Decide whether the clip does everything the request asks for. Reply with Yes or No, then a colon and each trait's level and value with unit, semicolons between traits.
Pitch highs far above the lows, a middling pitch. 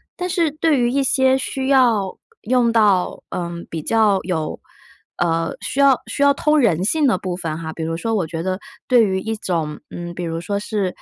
No: wide, 7.2 semitones; high, 200 Hz